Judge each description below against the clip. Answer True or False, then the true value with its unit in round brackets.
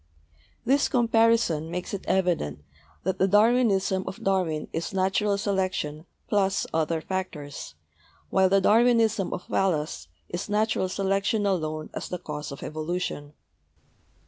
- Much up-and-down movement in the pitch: False (4.2 semitones)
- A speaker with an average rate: False (125 wpm)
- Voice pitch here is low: False (190 Hz)